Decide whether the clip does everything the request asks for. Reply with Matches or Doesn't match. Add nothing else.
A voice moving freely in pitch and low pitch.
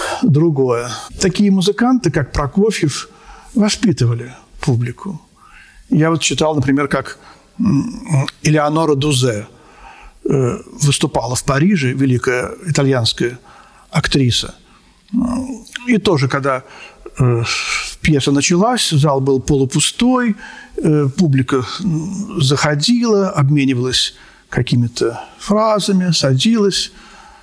Doesn't match